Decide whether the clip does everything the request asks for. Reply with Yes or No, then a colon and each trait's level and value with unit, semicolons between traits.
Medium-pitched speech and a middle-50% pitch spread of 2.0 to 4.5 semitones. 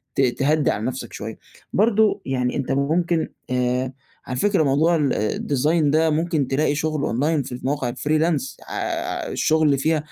Yes: medium, 145 Hz; average, 3.5 semitones